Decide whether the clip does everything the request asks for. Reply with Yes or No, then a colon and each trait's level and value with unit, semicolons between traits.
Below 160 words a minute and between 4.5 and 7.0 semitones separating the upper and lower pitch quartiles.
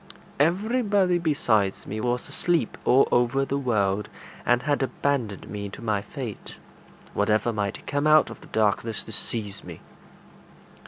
Yes: average, 145 wpm; wide, 5.6 semitones